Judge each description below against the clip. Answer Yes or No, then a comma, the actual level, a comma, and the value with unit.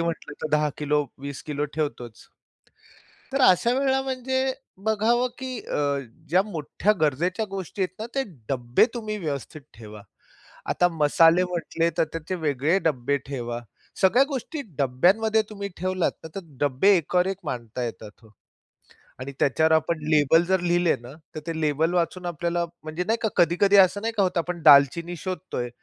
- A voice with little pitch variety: No, average, 5.0 semitones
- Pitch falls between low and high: Yes, medium, 170 Hz